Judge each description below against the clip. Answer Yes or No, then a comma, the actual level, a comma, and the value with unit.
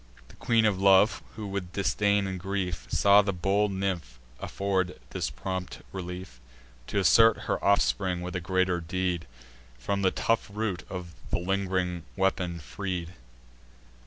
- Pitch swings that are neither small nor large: No, narrow, 1.9 semitones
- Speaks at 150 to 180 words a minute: No, average, 140 wpm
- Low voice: Yes, very low, 95 Hz